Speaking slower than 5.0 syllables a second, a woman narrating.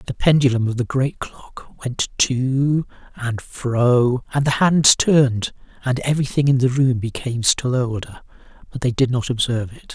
No: 4.5 syllables/s; male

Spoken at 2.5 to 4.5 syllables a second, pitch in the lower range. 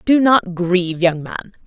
No: 4.1 syllables/s; high, 190 Hz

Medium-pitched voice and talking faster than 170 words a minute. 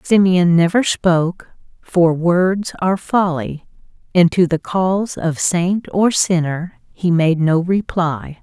No: medium, 175 Hz; slow, 135 wpm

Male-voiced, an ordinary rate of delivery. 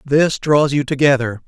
Yes: male; average, 165 wpm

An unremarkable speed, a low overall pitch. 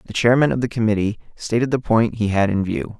No: fast, 240 wpm; low, 110 Hz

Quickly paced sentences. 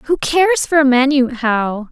No: average, 155 wpm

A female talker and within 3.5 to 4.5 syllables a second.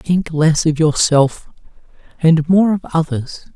No: male; 3.6 syllables/s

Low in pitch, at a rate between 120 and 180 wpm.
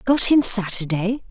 No: high, 220 Hz; average, 140 wpm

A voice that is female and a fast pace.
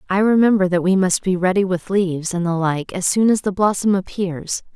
Yes: female; fast, 225 wpm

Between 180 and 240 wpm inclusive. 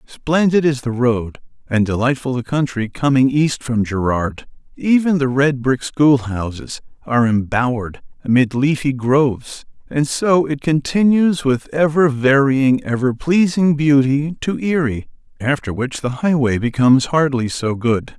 No: average, 140 wpm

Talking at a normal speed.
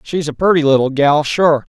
Yes: average, 170 wpm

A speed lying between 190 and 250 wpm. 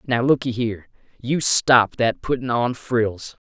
No: average, 155 wpm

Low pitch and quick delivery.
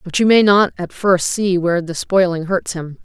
No: medium, 185 Hz; fast, 235 wpm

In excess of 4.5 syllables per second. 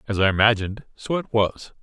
Yes: 5.8 syllables/s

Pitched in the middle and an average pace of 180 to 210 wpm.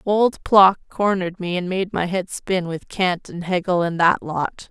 Yes: medium, 180 Hz; fast, 205 wpm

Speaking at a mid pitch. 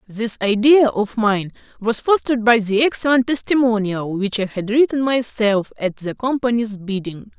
No: high, 225 Hz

